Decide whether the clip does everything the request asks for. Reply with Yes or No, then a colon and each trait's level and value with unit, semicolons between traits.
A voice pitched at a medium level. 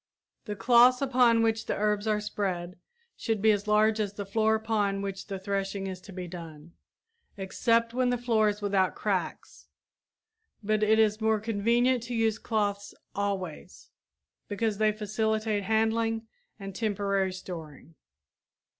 No: high, 210 Hz